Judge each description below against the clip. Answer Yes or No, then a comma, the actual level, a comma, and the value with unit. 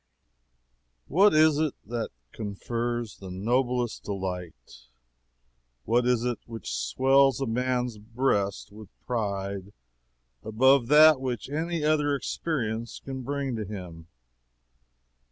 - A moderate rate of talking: No, slow, 110 wpm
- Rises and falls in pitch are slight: No, average, 4.8 semitones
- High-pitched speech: No, low, 120 Hz